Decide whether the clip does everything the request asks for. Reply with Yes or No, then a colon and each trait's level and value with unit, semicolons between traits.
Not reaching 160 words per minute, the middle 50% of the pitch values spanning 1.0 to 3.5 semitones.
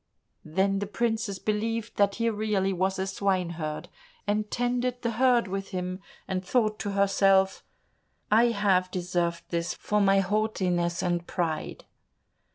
Yes: average, 140 wpm; average, 2.8 semitones